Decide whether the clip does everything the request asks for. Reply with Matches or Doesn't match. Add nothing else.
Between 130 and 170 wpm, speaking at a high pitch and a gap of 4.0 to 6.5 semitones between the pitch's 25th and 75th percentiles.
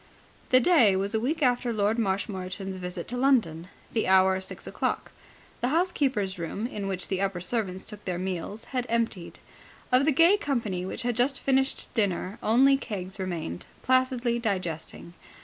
Matches